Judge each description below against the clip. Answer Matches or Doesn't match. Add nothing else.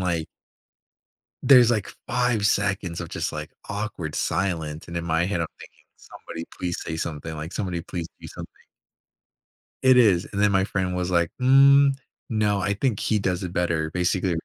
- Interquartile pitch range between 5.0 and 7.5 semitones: Doesn't match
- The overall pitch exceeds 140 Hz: Doesn't match